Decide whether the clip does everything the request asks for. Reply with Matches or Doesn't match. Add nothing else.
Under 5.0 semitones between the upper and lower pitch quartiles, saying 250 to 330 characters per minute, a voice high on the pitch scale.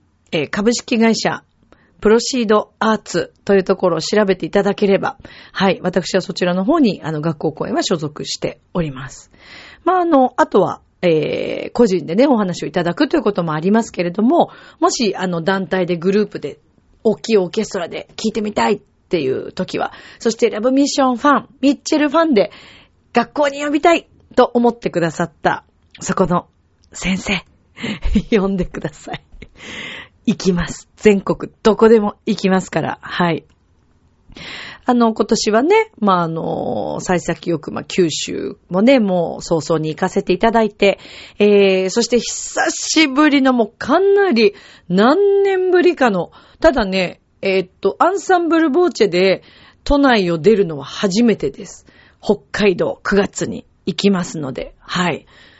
Doesn't match